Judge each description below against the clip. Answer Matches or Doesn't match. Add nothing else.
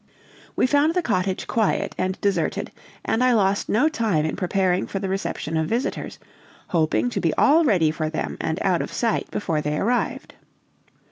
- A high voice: Matches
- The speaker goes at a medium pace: Matches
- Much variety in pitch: Matches